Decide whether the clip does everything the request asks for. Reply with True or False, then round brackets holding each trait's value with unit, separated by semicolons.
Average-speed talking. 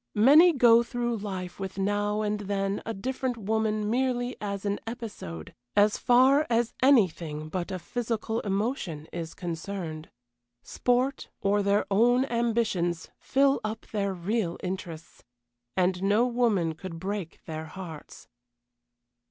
False (130 wpm)